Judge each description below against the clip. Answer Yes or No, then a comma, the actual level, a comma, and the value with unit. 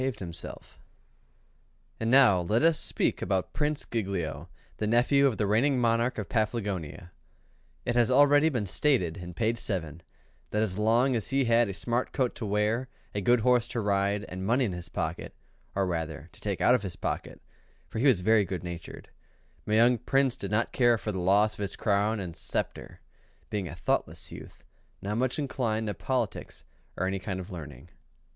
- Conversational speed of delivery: Yes, average, 185 wpm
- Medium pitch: No, low, 110 Hz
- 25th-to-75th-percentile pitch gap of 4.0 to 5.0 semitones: Yes, average, 4.3 semitones